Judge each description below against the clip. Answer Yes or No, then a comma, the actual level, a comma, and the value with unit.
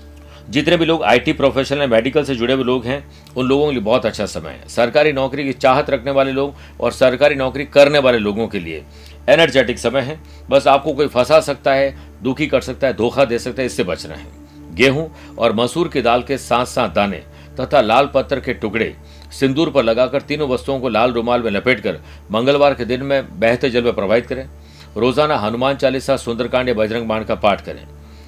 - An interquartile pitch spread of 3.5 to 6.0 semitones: Yes, average, 4.7 semitones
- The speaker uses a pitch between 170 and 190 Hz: No, low, 125 Hz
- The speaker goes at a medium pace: No, fast, 210 wpm